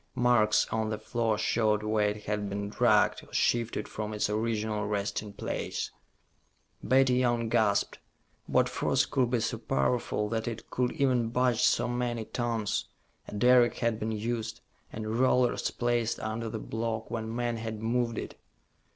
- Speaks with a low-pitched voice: Yes, low, 115 Hz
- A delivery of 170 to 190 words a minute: No, average, 160 wpm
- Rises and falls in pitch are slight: Yes, narrow, 2.0 semitones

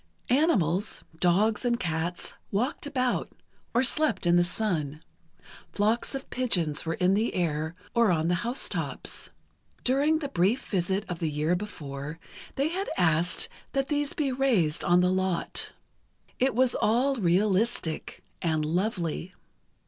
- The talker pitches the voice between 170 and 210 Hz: Yes, high, 190 Hz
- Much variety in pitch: Yes, wide, 6.8 semitones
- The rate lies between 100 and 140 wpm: Yes, slow, 135 wpm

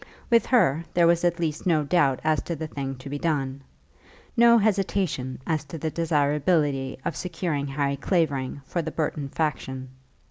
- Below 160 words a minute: No, average, 170 wpm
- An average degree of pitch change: Yes, average, 3.7 semitones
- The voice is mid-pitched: Yes, medium, 155 Hz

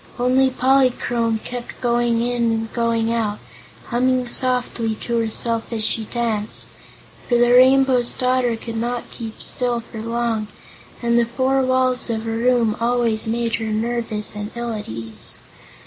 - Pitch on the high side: Yes, high, 235 Hz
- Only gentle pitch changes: Yes, narrow, 1.6 semitones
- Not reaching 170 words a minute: Yes, average, 150 wpm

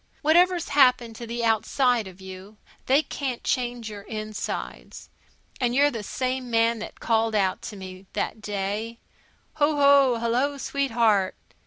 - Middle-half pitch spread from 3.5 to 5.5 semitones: Yes, average, 3.8 semitones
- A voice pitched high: Yes, high, 235 Hz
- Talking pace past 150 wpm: No, average, 145 wpm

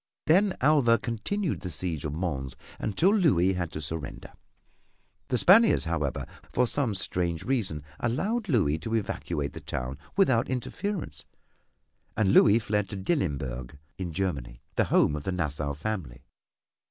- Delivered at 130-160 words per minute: Yes, average, 140 wpm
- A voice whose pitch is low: Yes, very low, 95 Hz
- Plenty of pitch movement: Yes, wide, 9.0 semitones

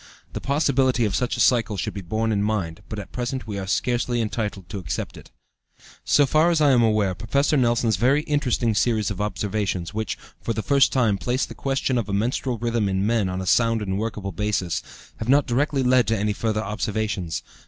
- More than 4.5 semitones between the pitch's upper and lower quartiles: No, average, 3.5 semitones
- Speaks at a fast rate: Yes, fast, 210 wpm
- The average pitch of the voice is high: No, low, 110 Hz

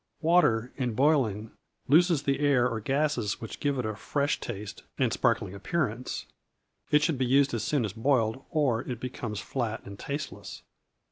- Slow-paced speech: No, average, 165 wpm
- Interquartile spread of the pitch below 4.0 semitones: No, average, 4.4 semitones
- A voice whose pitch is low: Yes, low, 125 Hz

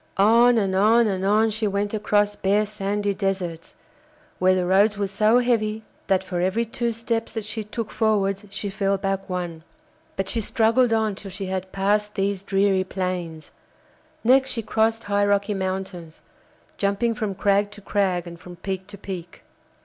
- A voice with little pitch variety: Yes, narrow, 2.2 semitones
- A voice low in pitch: No, high, 200 Hz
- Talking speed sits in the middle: Yes, average, 170 wpm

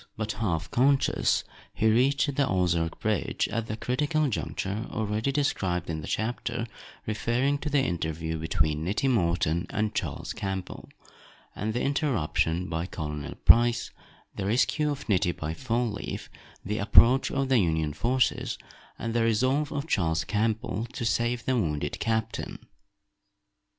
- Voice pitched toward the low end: Yes, low, 110 Hz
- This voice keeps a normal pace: Yes, average, 145 wpm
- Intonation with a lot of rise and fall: Yes, wide, 6.4 semitones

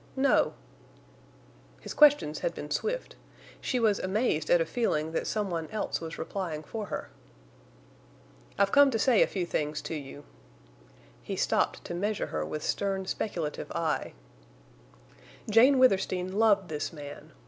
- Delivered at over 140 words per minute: Yes, average, 150 wpm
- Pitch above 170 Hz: Yes, medium, 185 Hz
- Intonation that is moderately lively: No, wide, 5.7 semitones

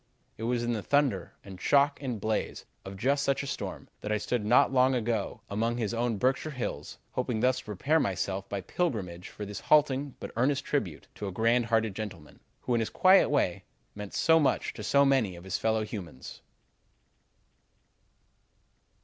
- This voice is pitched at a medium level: No, low, 115 Hz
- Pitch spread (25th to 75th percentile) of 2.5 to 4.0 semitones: No, average, 4.8 semitones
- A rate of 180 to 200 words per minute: Yes, average, 185 wpm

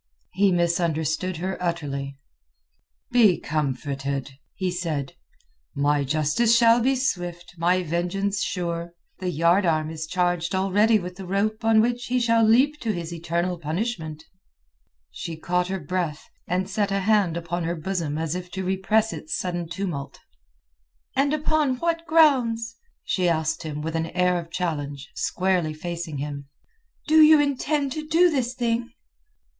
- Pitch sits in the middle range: Yes, medium, 180 Hz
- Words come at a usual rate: Yes, average, 150 wpm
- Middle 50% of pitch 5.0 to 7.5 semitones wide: Yes, wide, 5.6 semitones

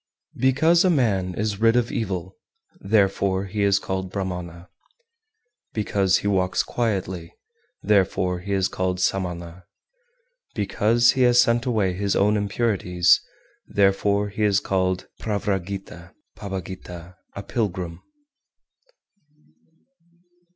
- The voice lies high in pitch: No, low, 100 Hz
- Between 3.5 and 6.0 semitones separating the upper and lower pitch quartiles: No, narrow, 2.5 semitones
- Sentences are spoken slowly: Yes, slow, 110 wpm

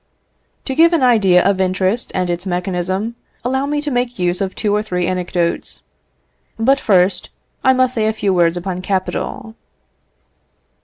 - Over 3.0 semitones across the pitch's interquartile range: Yes, average, 5.2 semitones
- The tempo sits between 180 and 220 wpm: No, average, 160 wpm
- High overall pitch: Yes, high, 195 Hz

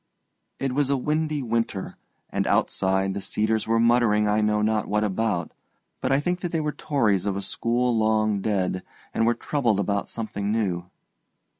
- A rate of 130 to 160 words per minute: No, average, 175 wpm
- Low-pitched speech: Yes, low, 110 Hz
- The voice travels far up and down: No, average, 3.4 semitones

